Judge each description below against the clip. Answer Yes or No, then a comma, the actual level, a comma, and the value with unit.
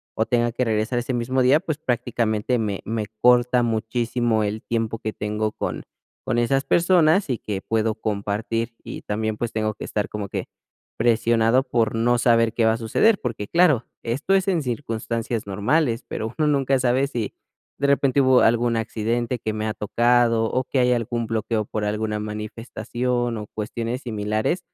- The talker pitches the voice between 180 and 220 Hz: No, low, 115 Hz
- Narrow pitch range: Yes, narrow, 2.3 semitones